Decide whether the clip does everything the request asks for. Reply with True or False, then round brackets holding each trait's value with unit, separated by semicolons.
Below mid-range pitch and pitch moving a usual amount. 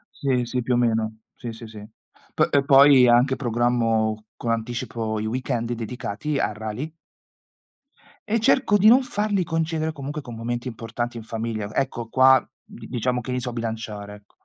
True (120 Hz; 3.2 semitones)